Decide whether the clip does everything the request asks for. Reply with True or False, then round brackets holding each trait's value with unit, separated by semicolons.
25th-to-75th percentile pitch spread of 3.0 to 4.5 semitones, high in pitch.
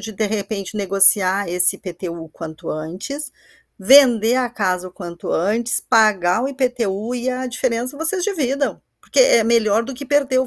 False (5.2 semitones; 225 Hz)